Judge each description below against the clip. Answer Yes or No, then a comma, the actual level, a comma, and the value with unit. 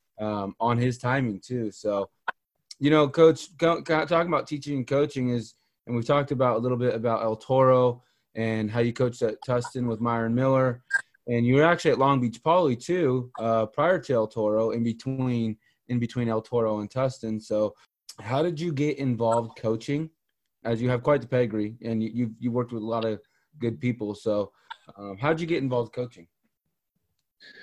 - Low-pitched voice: Yes, low, 120 Hz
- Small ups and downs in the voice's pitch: No, average, 3.2 semitones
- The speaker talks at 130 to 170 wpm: No, average, 195 wpm